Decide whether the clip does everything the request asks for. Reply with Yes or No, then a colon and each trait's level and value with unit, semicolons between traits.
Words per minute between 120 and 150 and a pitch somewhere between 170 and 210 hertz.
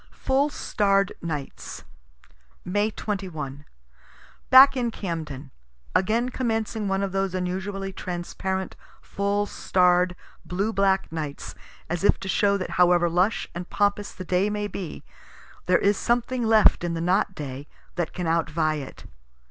Yes: average, 140 wpm; high, 190 Hz